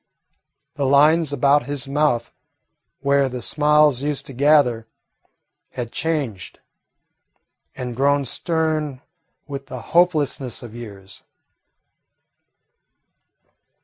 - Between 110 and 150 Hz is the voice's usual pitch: Yes, medium, 140 Hz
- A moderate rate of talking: No, slow, 90 wpm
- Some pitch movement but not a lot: Yes, average, 3.3 semitones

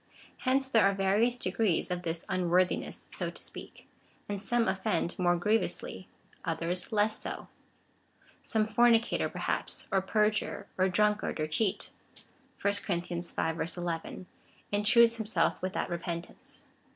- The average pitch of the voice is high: Yes, high, 195 Hz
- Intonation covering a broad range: No, average, 3.8 semitones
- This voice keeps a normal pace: No, slow, 130 wpm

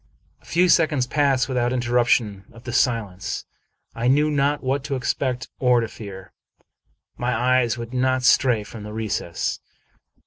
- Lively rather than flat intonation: No, narrow, 2.4 semitones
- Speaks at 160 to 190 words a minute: No, average, 150 wpm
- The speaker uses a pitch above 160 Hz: No, low, 125 Hz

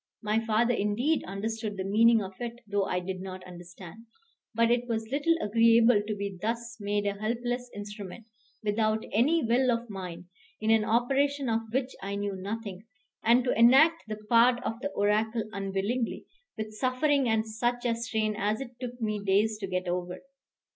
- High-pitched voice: Yes, high, 220 Hz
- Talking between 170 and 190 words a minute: Yes, average, 175 wpm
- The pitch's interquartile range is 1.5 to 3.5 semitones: Yes, average, 2.9 semitones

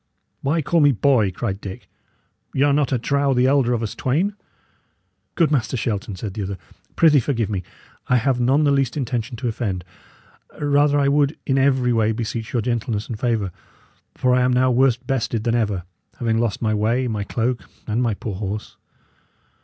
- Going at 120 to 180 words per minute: No, average, 190 wpm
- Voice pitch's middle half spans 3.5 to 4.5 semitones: Yes, average, 3.8 semitones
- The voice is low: Yes, low, 120 Hz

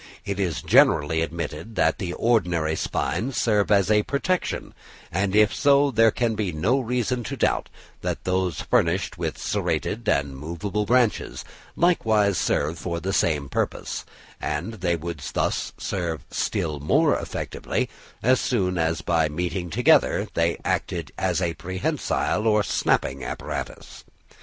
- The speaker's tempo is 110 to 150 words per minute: Yes, average, 140 wpm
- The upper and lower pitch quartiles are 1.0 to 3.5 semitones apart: No, average, 4.9 semitones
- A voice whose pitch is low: Yes, very low, 90 Hz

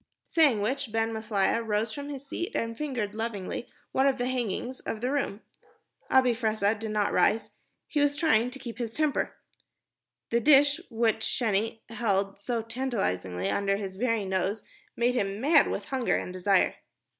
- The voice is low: No, high, 230 Hz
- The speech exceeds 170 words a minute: No, average, 165 wpm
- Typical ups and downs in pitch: Yes, average, 3.9 semitones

